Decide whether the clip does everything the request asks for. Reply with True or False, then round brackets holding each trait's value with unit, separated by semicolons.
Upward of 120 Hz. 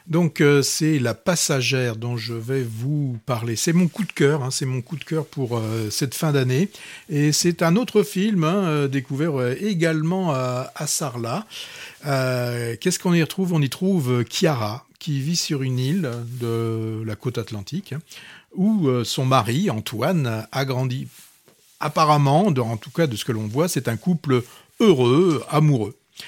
True (140 Hz)